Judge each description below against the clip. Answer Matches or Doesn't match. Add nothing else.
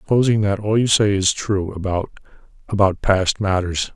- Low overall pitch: Matches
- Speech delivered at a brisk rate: Doesn't match